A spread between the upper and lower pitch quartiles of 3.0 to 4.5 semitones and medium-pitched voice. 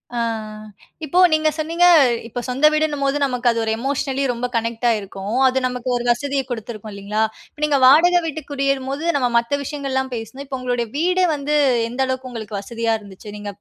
No: average, 3.6 semitones; very high, 260 Hz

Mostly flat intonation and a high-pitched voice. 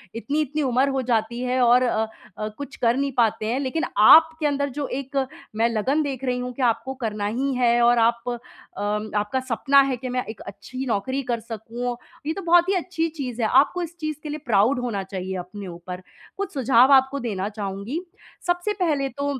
No: average, 4.1 semitones; very high, 250 Hz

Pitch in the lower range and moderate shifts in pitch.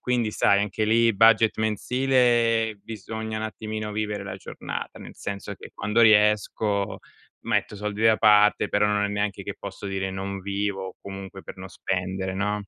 No: low, 105 Hz; narrow, 1.9 semitones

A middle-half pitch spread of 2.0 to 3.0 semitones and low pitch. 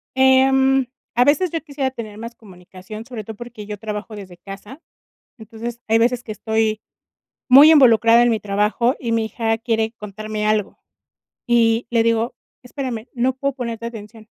No: narrow, 2.5 semitones; high, 230 Hz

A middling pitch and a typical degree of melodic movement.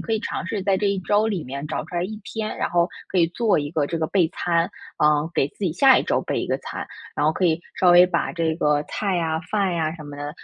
Yes: medium, 175 Hz; average, 3.9 semitones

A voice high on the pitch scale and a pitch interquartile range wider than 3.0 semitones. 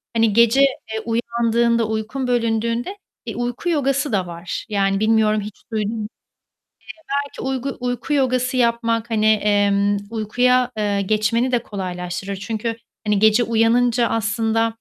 No: high, 225 Hz; narrow, 2.4 semitones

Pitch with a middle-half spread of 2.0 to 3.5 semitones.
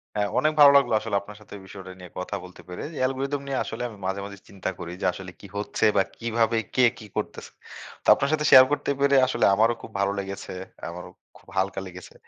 No: average, 5.1 semitones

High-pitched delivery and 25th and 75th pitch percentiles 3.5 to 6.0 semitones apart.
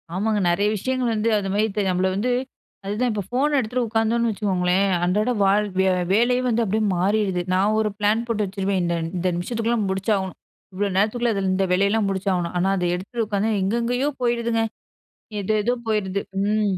No: high, 210 Hz; average, 3.1 semitones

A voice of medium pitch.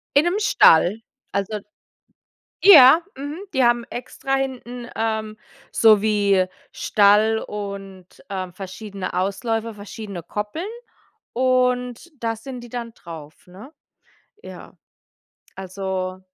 No: high, 220 Hz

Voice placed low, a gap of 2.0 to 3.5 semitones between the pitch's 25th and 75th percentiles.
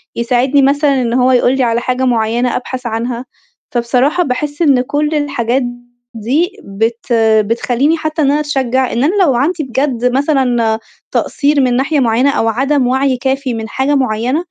No: very high, 260 Hz; average, 3.0 semitones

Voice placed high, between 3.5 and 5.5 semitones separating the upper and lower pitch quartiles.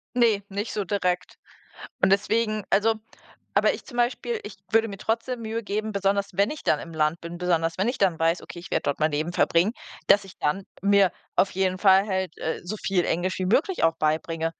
Yes: high, 195 Hz; average, 3.9 semitones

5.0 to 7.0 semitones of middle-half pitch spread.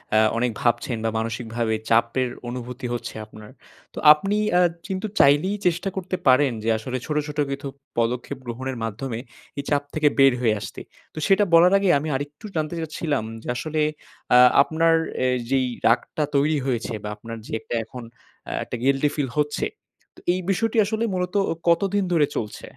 Yes: average, 5.3 semitones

